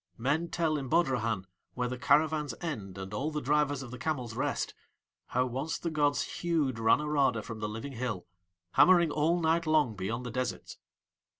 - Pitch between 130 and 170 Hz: Yes, low, 135 Hz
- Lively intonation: No, average, 5.0 semitones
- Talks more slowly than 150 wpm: No, average, 175 wpm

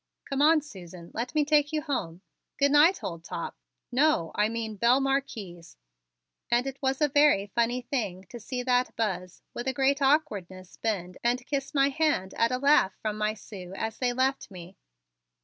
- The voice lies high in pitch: Yes, high, 245 Hz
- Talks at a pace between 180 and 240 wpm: Yes, average, 185 wpm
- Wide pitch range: Yes, wide, 6.0 semitones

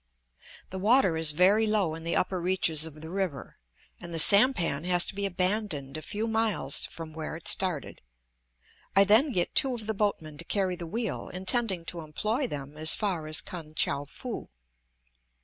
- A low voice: No, medium, 180 Hz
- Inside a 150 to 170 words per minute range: No, average, 185 wpm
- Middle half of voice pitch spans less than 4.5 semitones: No, average, 4.9 semitones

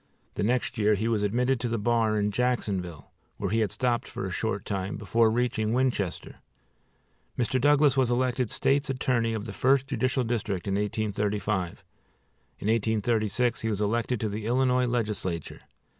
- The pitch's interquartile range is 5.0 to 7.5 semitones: No, average, 3.2 semitones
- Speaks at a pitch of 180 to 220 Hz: No, low, 115 Hz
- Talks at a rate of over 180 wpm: No, average, 165 wpm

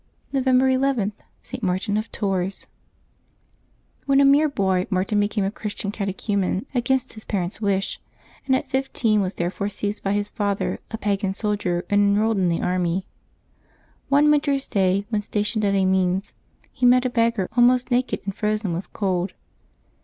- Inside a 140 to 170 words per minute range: Yes, average, 165 wpm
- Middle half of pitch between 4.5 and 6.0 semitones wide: No, average, 4.0 semitones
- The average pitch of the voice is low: No, high, 205 Hz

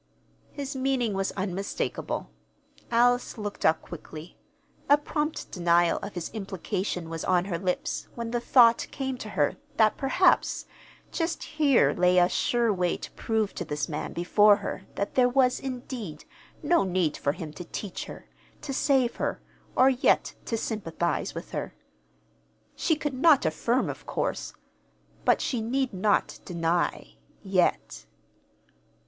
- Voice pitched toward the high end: Yes, high, 210 Hz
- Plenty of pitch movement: Yes, wide, 6.4 semitones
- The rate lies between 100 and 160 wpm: Yes, average, 145 wpm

